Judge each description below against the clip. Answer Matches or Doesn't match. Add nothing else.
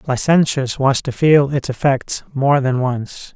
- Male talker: Matches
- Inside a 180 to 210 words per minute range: Doesn't match